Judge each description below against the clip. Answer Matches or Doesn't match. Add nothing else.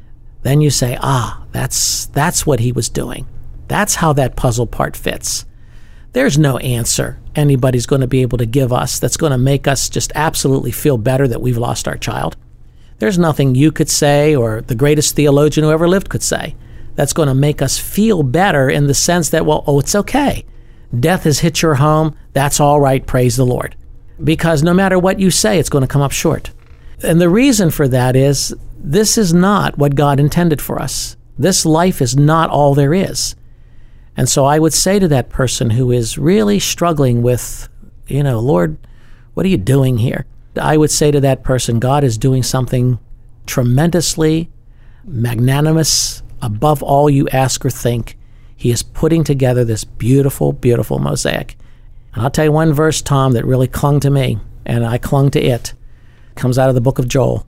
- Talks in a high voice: Doesn't match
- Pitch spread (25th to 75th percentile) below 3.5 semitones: Doesn't match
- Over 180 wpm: Matches